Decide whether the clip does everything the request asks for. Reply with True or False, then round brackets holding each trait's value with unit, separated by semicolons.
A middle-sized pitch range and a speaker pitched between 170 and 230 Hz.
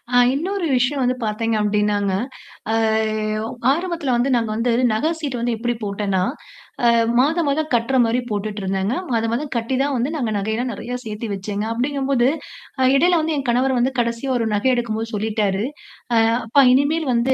False (4.1 semitones; 240 Hz)